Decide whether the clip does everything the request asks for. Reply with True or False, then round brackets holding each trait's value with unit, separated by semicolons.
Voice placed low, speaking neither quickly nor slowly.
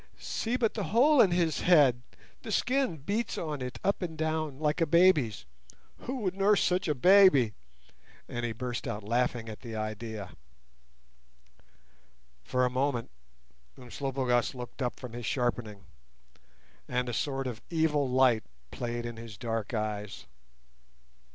True (130 Hz; 145 wpm)